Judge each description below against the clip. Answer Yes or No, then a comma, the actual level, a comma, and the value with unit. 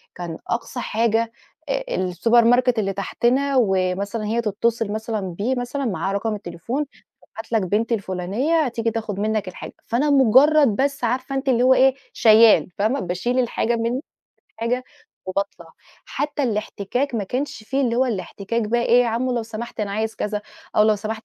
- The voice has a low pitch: No, high, 230 Hz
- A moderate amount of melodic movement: Yes, average, 3.4 semitones